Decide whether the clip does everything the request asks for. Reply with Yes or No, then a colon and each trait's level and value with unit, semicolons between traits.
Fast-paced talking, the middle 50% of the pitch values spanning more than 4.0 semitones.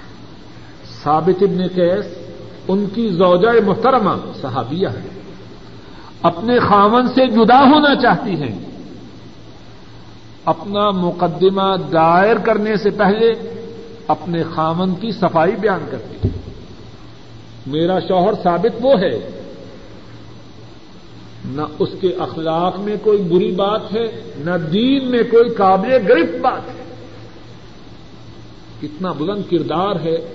No: slow, 110 wpm; average, 5.2 semitones